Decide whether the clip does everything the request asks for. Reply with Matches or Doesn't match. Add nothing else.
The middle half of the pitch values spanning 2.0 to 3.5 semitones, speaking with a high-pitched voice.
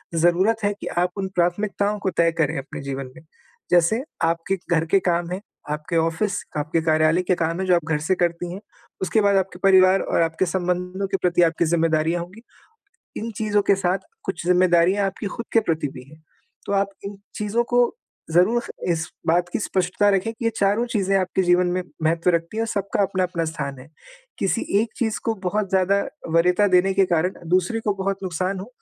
Doesn't match